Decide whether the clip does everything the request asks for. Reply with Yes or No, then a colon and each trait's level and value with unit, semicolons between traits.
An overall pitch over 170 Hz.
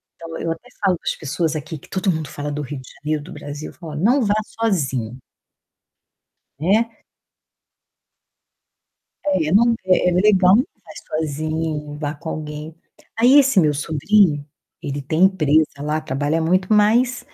No: medium, 160 Hz